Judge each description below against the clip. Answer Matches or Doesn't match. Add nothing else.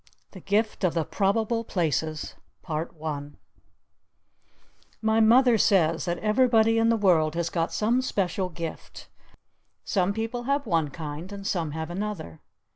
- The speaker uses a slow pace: Matches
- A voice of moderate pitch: Doesn't match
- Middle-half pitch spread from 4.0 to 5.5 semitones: Matches